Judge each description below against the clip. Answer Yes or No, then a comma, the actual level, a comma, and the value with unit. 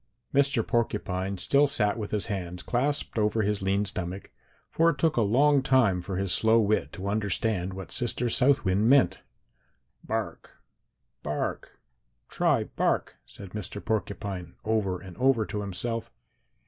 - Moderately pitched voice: No, low, 105 Hz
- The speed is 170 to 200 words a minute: No, average, 150 wpm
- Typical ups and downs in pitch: Yes, average, 3.9 semitones